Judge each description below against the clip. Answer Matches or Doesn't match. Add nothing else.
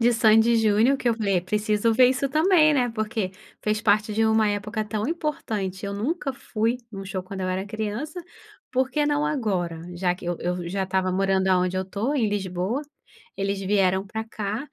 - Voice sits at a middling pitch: Doesn't match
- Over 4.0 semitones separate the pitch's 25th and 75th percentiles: Doesn't match